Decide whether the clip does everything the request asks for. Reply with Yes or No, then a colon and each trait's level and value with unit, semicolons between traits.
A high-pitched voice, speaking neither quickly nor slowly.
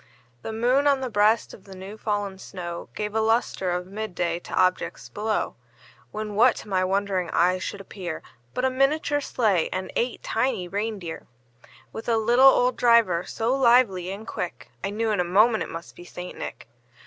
Yes: high, 210 Hz; average, 195 wpm